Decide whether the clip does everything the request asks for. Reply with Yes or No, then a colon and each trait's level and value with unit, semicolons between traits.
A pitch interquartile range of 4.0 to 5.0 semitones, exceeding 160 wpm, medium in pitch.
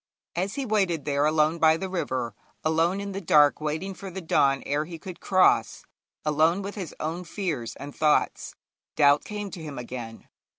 Yes: average, 4.4 semitones; average, 180 wpm; medium, 160 Hz